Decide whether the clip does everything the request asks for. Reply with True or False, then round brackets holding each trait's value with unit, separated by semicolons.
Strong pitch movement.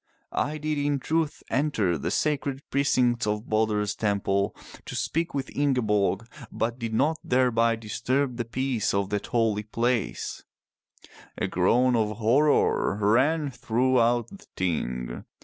False (4.4 semitones)